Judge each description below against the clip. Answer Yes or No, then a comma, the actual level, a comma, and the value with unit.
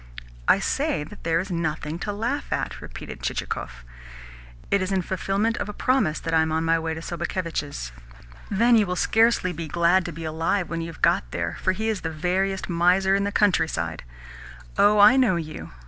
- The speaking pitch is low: No, medium, 175 Hz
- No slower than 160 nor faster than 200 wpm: Yes, average, 195 wpm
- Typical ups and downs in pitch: Yes, average, 3.8 semitones